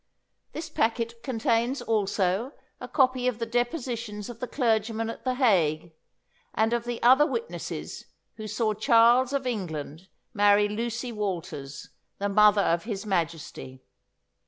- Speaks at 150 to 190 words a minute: No, slow, 135 wpm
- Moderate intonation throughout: Yes, average, 3.2 semitones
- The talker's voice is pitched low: No, high, 225 Hz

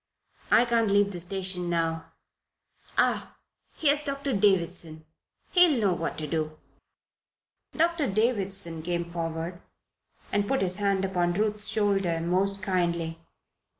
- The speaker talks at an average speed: No, slow, 120 wpm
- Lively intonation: No, average, 3.5 semitones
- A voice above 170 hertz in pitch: Yes, high, 190 Hz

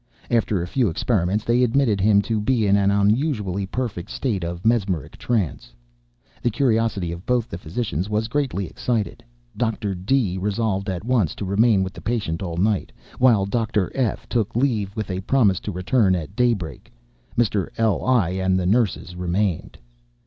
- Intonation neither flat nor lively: Yes, average, 4.0 semitones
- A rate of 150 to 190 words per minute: Yes, average, 165 wpm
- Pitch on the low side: Yes, low, 105 Hz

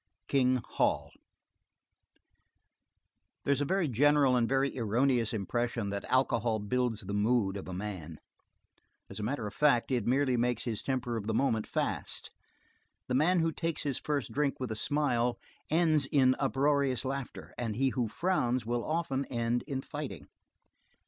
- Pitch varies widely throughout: No, average, 3.5 semitones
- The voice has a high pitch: No, low, 125 Hz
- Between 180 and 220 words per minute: No, average, 160 wpm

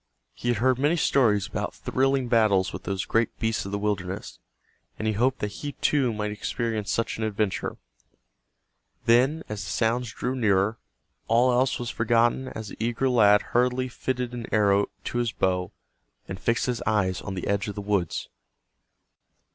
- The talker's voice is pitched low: Yes, low, 115 Hz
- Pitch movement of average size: Yes, average, 3.3 semitones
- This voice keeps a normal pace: Yes, average, 175 wpm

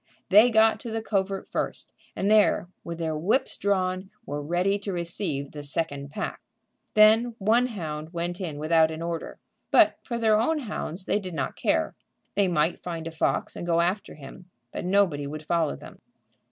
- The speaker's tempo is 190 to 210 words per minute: No, average, 180 wpm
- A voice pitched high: No, medium, 180 Hz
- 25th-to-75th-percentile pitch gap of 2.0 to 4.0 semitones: No, average, 4.5 semitones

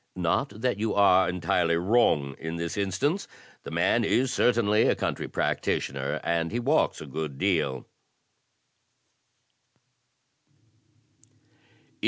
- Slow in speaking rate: Yes, slow, 110 wpm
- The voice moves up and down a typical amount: No, wide, 5.8 semitones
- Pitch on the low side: Yes, very low, 95 Hz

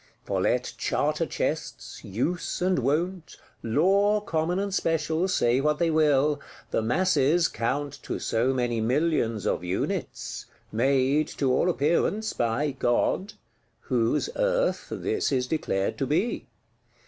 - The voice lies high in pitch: No, medium, 150 Hz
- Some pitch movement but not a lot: No, wide, 6.0 semitones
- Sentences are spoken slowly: Yes, slow, 125 wpm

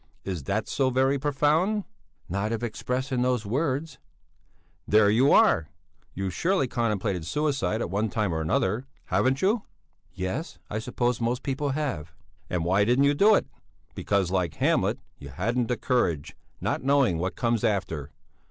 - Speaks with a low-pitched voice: Yes, low, 120 Hz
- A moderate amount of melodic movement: No, wide, 6.1 semitones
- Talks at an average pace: Yes, average, 160 wpm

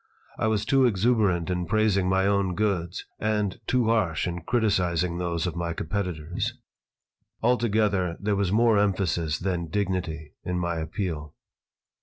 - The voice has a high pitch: No, very low, 95 Hz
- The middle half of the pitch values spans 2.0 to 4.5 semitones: Yes, average, 3.6 semitones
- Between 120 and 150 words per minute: Yes, average, 140 wpm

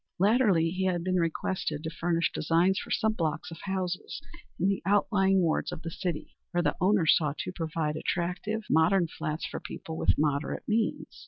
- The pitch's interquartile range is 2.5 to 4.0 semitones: Yes, average, 3.0 semitones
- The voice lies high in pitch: No, medium, 175 Hz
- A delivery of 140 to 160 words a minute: No, average, 180 wpm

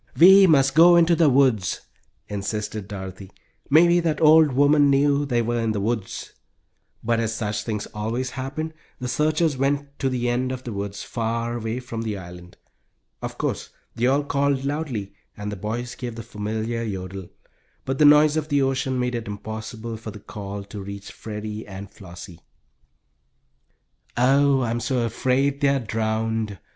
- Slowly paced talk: No, average, 170 wpm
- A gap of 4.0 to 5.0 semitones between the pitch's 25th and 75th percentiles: Yes, average, 4.7 semitones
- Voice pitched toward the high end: No, low, 120 Hz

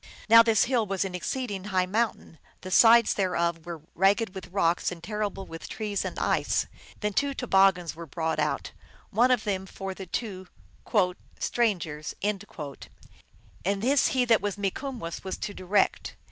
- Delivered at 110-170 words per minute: Yes, average, 165 wpm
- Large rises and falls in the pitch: No, average, 3.6 semitones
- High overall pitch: Yes, high, 195 Hz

